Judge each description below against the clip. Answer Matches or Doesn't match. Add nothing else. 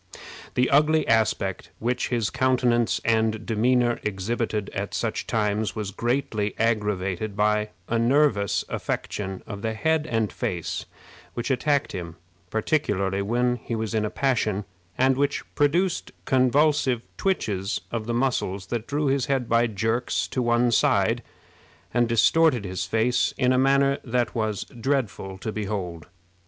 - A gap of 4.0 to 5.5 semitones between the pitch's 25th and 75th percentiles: Doesn't match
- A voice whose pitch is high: Doesn't match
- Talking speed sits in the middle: Matches